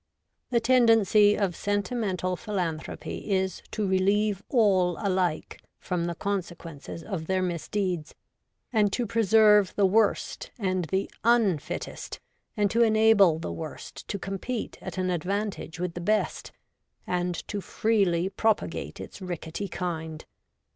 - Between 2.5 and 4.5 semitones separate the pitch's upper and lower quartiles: Yes, average, 3.1 semitones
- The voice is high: Yes, high, 195 Hz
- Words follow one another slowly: Yes, slow, 130 wpm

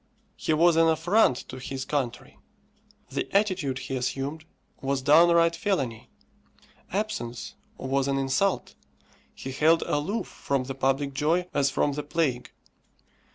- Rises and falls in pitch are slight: No, average, 3.9 semitones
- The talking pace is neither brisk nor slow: No, slow, 130 wpm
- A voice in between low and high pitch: Yes, medium, 145 Hz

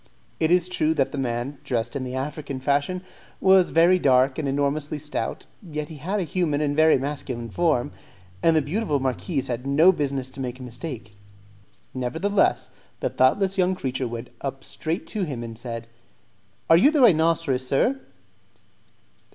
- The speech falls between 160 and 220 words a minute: Yes, average, 165 wpm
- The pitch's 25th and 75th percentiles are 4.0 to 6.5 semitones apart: Yes, average, 4.3 semitones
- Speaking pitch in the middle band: Yes, medium, 145 Hz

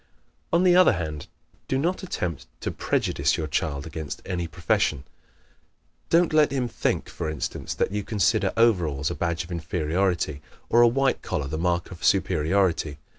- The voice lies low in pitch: Yes, very low, 90 Hz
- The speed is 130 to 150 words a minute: No, average, 165 wpm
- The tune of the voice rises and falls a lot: Yes, wide, 6.8 semitones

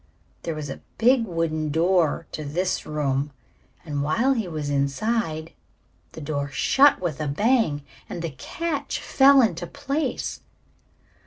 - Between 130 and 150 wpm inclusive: Yes, average, 140 wpm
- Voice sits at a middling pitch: Yes, medium, 165 Hz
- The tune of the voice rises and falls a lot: Yes, wide, 7.5 semitones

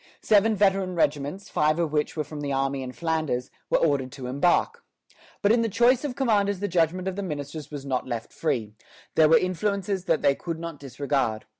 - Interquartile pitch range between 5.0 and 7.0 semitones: Yes, wide, 5.6 semitones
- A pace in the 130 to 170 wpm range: No, average, 200 wpm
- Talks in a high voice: No, medium, 160 Hz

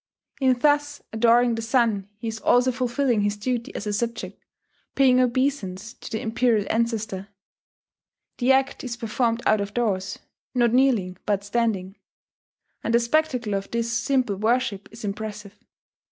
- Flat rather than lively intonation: No, average, 3.2 semitones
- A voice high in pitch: Yes, high, 230 Hz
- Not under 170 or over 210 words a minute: No, average, 150 wpm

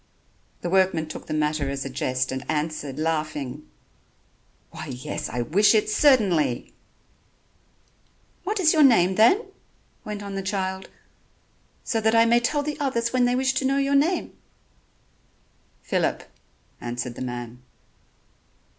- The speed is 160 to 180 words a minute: No, average, 140 wpm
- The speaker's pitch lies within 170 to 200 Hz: Yes, high, 190 Hz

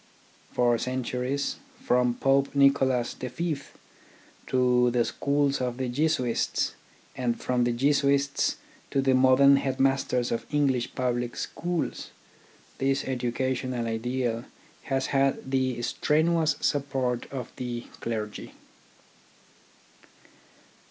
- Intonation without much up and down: Yes, narrow, 2.1 semitones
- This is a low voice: Yes, low, 130 Hz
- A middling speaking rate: No, slow, 100 wpm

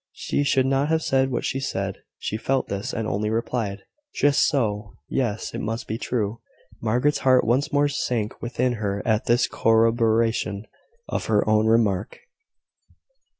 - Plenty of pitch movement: No, average, 3.4 semitones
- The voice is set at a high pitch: No, low, 115 Hz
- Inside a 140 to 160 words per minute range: Yes, average, 155 wpm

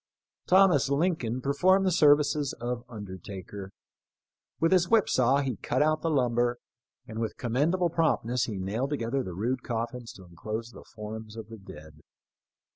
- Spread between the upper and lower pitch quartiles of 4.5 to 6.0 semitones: Yes, average, 5.1 semitones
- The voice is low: Yes, low, 125 Hz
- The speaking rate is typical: Yes, average, 160 wpm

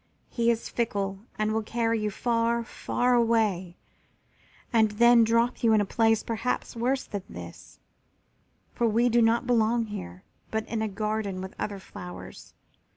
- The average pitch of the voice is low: No, high, 225 Hz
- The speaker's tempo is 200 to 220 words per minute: No, average, 155 wpm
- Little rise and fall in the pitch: Yes, narrow, 1.9 semitones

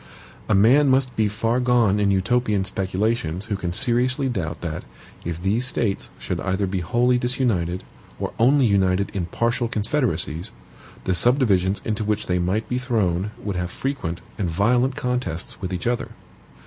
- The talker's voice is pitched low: Yes, low, 105 Hz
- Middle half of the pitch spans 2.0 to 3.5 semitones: No, average, 4.9 semitones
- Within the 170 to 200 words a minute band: No, average, 160 wpm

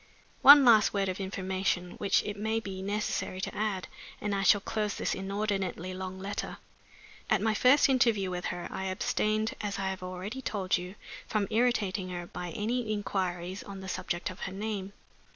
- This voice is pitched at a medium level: No, high, 195 Hz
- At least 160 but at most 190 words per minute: Yes, average, 180 wpm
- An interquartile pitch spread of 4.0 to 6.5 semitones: No, narrow, 2.4 semitones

